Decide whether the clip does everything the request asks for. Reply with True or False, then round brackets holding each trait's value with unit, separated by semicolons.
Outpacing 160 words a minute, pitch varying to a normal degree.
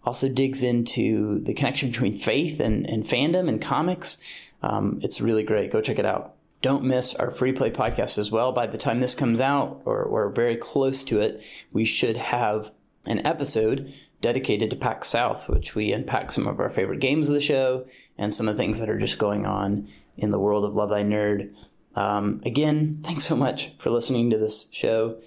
True (205 wpm; 4.1 semitones)